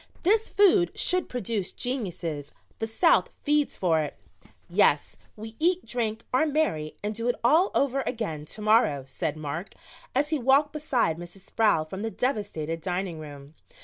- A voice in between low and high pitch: No, high, 220 Hz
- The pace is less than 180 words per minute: Yes, average, 160 wpm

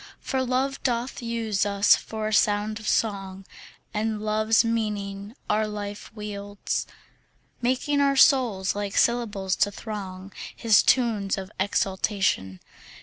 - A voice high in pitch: Yes, high, 210 Hz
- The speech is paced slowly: Yes, slow, 125 wpm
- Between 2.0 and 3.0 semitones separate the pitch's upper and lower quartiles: Yes, narrow, 2.5 semitones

